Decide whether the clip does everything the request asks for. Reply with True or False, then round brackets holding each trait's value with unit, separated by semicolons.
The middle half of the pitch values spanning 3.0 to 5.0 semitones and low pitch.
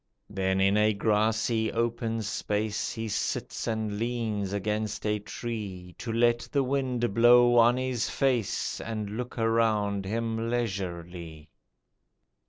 False (2.5 semitones; 110 Hz)